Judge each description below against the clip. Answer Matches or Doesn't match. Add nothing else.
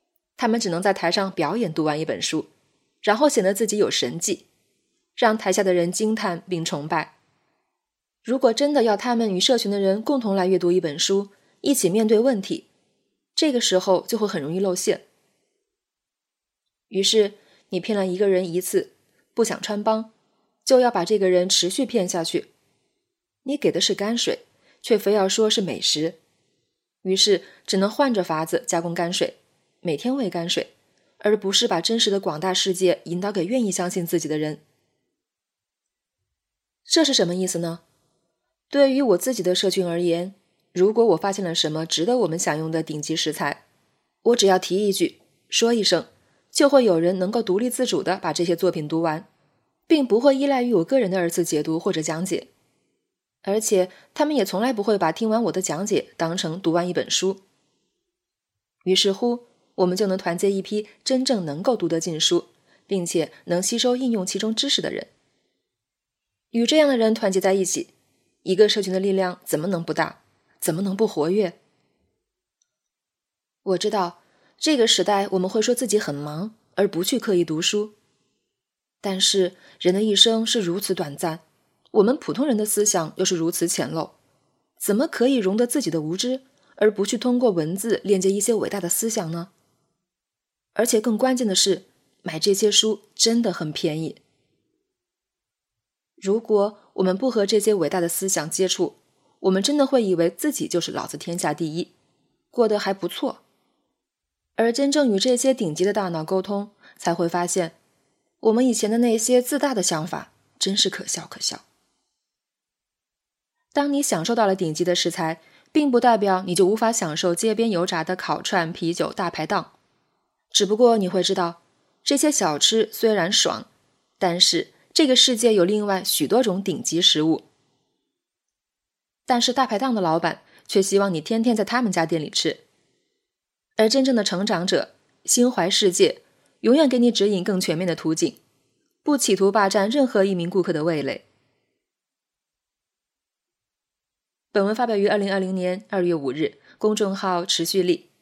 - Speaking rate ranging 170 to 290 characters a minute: Matches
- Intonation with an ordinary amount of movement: Matches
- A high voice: Matches